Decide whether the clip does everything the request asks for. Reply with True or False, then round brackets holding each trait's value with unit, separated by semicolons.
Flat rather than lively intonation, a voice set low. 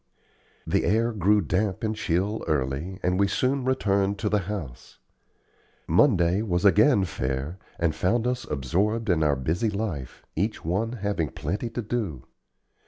False (4.8 semitones; 100 Hz)